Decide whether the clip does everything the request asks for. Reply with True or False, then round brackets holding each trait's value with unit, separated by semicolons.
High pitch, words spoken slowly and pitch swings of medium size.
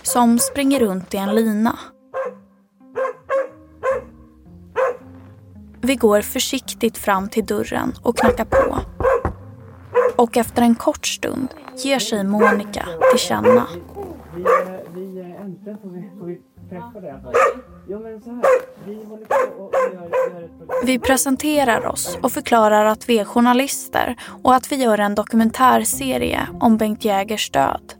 True (235 Hz; 95 wpm; 4.3 semitones)